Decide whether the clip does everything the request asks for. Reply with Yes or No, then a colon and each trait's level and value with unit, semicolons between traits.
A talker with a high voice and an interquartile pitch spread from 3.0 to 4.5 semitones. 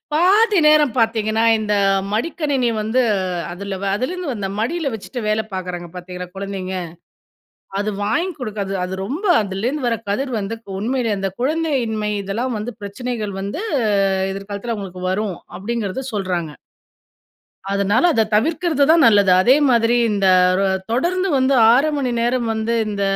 No: high, 225 Hz; average, 5.0 semitones